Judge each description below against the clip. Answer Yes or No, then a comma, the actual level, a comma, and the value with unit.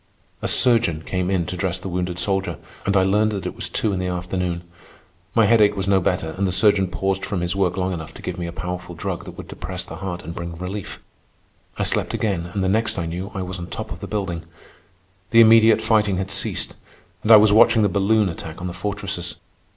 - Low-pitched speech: Yes, very low, 95 Hz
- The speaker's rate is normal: No, fast, 235 wpm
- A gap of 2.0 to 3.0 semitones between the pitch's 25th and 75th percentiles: Yes, narrow, 2.6 semitones